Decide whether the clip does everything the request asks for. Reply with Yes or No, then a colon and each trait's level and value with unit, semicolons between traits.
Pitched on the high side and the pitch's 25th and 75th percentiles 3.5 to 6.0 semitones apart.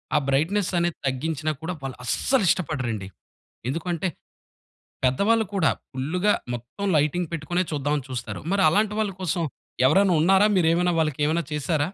No: medium, 160 Hz; average, 4.5 semitones